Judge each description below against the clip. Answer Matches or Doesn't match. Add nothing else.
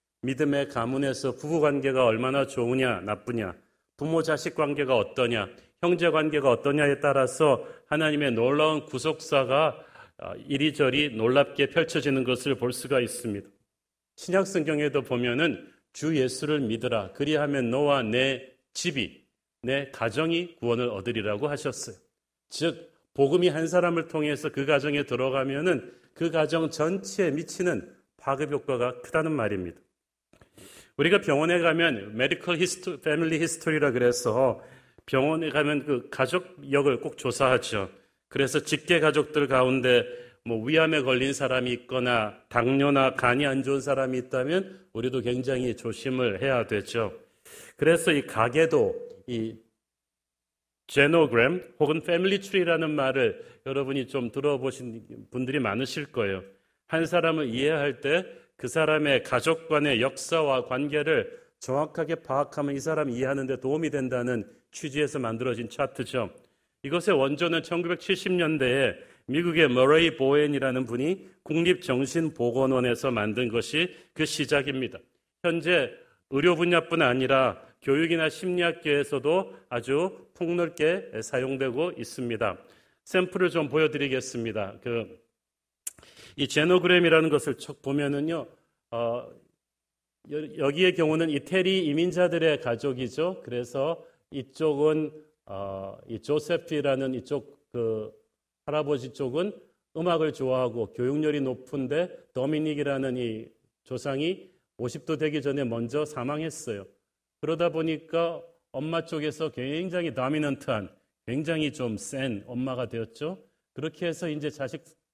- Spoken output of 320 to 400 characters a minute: Doesn't match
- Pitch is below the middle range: Doesn't match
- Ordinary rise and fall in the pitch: Matches